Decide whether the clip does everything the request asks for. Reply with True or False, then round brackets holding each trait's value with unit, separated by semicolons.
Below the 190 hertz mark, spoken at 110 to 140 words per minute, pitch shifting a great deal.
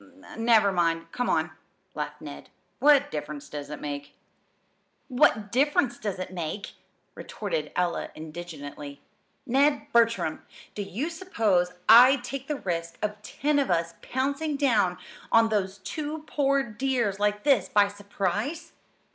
False (210 Hz; 135 wpm; 7.5 semitones)